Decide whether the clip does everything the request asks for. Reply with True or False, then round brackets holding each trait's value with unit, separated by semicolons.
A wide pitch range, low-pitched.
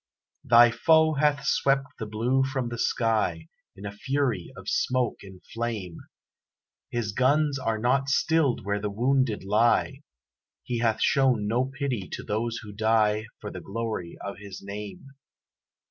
False (4.3 semitones; 115 Hz)